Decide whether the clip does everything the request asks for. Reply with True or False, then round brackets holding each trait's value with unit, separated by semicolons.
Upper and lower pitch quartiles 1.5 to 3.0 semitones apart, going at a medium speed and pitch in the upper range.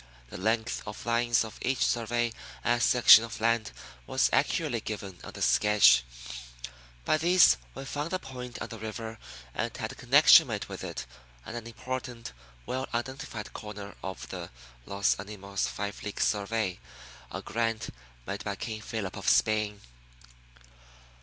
False (2.6 semitones; 155 wpm; 115 Hz)